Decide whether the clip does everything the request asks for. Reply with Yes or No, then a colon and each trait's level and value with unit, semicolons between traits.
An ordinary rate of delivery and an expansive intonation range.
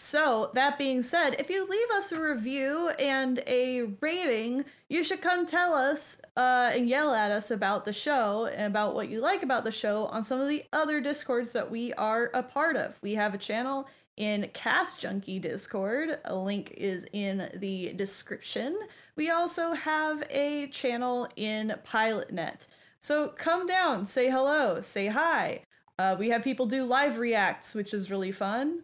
Yes: average, 175 wpm; wide, 6.1 semitones